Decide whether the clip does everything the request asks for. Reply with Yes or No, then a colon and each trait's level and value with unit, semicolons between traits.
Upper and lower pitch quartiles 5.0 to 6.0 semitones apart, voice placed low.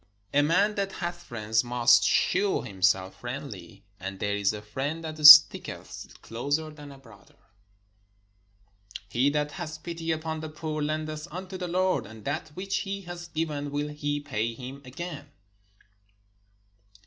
No: wide, 5.5 semitones; medium, 150 Hz